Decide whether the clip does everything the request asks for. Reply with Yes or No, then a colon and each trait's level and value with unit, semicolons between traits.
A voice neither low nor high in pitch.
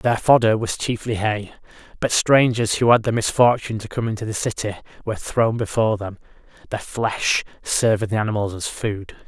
No: low, 110 Hz